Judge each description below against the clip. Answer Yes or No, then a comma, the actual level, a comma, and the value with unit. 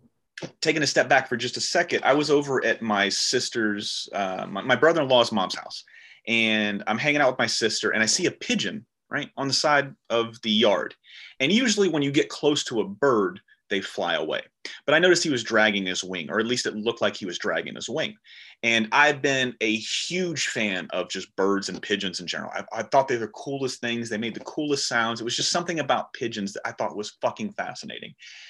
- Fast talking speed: Yes, fast, 225 wpm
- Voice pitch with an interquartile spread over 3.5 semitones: Yes, average, 5.0 semitones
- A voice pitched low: Yes, low, 115 Hz